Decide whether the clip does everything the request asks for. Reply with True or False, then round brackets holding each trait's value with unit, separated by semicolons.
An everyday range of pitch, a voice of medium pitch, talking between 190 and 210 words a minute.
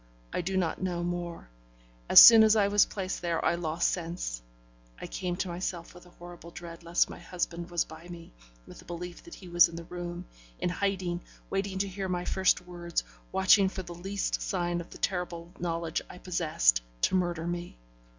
False (1.5 semitones; 175 Hz; 200 wpm)